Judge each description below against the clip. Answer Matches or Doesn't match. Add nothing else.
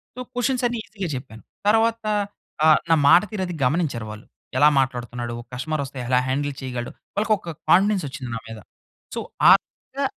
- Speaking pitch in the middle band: Matches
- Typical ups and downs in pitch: Doesn't match